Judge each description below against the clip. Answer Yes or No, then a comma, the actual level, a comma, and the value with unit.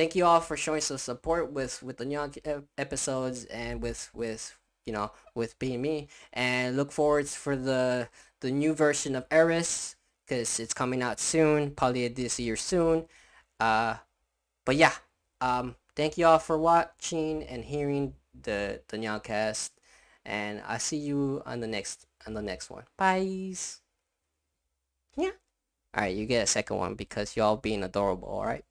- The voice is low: Yes, low, 130 Hz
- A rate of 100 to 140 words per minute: No, average, 165 wpm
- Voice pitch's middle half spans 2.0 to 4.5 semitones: No, average, 5.1 semitones